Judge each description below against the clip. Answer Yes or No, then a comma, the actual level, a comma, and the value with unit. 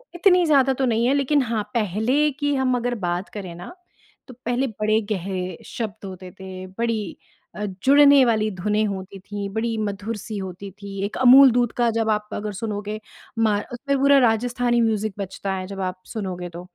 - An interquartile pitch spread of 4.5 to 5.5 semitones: No, average, 3.8 semitones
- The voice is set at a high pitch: Yes, high, 215 Hz